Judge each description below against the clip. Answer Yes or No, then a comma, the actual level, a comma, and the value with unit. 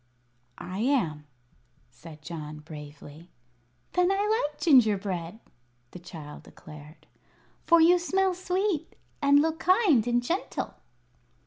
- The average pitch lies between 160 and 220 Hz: No, high, 240 Hz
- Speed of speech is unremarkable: No, slow, 110 wpm